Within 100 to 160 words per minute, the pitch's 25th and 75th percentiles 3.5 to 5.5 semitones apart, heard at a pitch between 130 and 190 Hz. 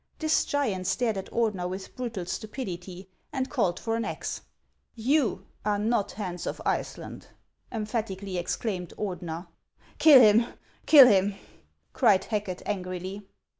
No: average, 150 wpm; average, 4.0 semitones; high, 205 Hz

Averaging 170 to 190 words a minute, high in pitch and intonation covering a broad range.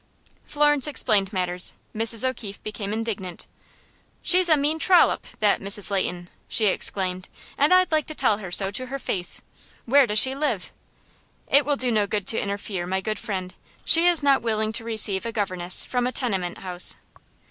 Yes: average, 180 wpm; high, 215 Hz; wide, 5.8 semitones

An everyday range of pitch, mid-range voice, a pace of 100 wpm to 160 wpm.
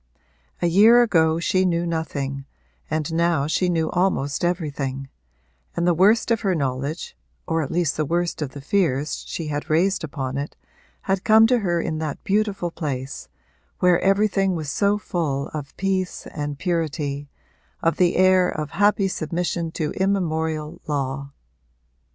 Yes: average, 4.1 semitones; medium, 165 Hz; average, 155 wpm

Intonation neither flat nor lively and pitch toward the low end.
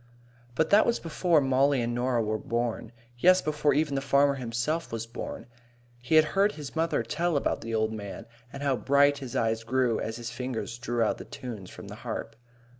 Yes: average, 4.3 semitones; low, 130 Hz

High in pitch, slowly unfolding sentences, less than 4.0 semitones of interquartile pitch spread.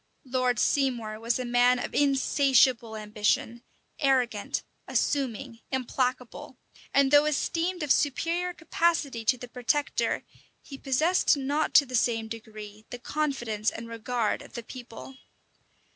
Yes: very high, 255 Hz; slow, 130 wpm; average, 3.4 semitones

